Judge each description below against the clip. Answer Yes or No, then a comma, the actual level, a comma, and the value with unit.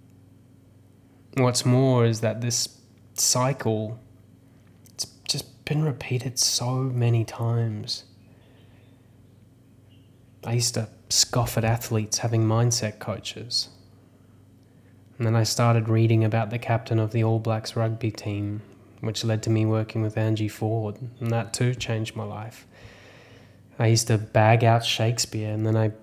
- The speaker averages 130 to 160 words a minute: Yes, slow, 135 wpm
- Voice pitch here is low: Yes, low, 115 Hz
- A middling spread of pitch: No, narrow, 1.9 semitones